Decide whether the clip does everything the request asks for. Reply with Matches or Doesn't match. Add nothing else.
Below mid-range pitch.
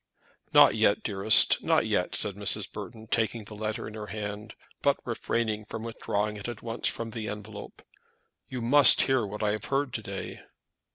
Matches